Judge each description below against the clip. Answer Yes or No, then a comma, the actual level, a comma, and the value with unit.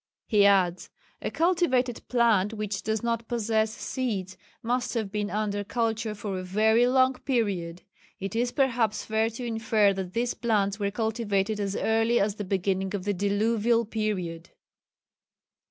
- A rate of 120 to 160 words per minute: Yes, average, 155 wpm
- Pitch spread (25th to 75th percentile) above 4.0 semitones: No, average, 2.7 semitones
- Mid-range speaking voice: No, high, 215 Hz